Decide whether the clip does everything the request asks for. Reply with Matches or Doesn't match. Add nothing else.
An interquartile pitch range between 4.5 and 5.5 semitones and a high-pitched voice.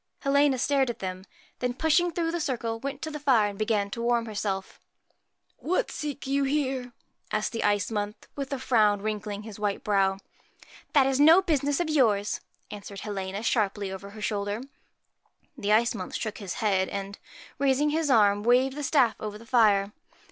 Matches